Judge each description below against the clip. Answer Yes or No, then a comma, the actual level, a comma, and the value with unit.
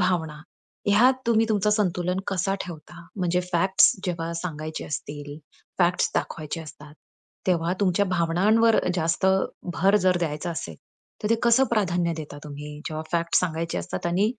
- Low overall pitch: No, medium, 175 Hz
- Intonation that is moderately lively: Yes, average, 3.2 semitones